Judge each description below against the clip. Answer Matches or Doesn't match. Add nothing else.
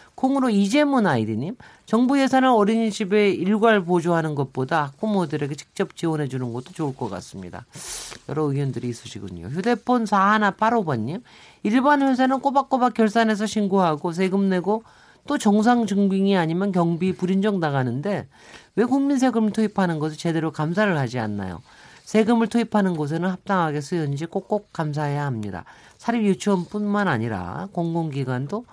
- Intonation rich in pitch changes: Matches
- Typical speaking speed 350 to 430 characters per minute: Matches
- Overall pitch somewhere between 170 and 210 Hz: Matches